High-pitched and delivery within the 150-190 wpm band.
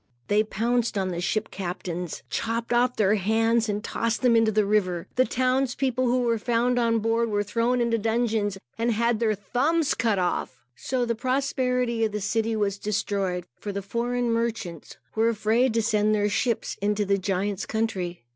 Yes: high, 225 Hz; average, 185 wpm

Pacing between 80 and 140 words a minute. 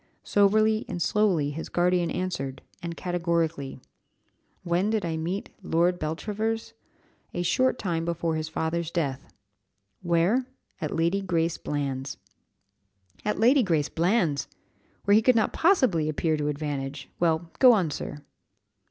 Yes: slow, 135 wpm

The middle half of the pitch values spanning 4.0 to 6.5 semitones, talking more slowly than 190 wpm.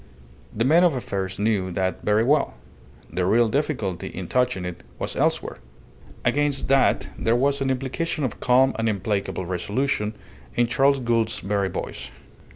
Yes: wide, 5.6 semitones; average, 155 wpm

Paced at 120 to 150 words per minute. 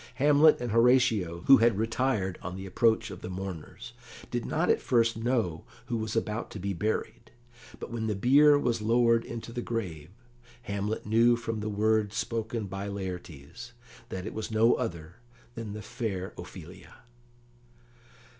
No: average, 160 wpm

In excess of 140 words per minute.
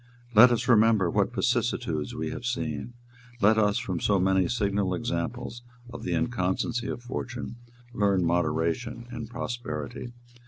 No: slow, 135 wpm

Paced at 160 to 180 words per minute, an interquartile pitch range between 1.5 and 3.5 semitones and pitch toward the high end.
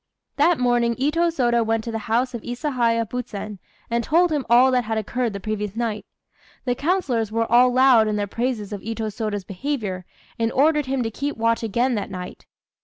No: average, 195 wpm; average, 2.9 semitones; high, 235 Hz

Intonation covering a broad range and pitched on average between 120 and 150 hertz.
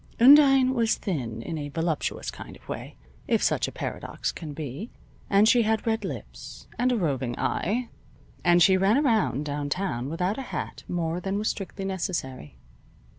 No: wide, 7.0 semitones; medium, 185 Hz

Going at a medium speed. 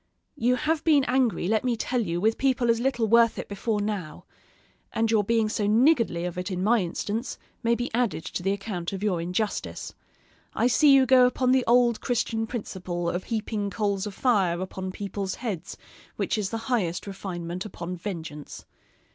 Yes: average, 185 wpm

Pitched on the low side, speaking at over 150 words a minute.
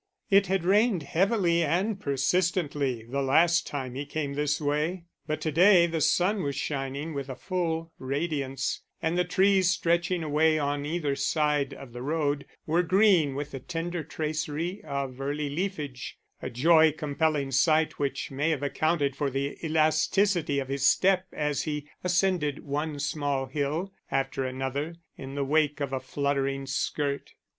No: medium, 150 Hz; average, 160 wpm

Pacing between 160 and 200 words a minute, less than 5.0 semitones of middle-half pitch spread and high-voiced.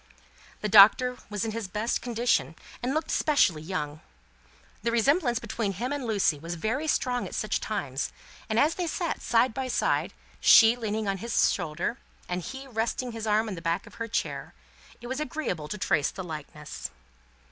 No: average, 185 wpm; wide, 5.4 semitones; high, 220 Hz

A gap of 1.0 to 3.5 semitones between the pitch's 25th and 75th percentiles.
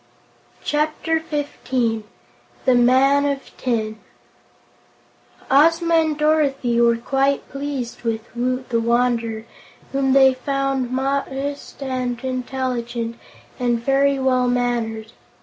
Yes: narrow, 2.6 semitones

